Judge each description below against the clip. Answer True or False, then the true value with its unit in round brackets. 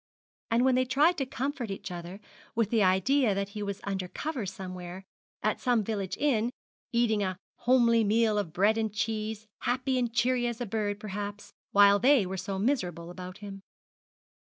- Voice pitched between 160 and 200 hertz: False (215 Hz)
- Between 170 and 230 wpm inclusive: True (180 wpm)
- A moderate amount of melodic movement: True (3.7 semitones)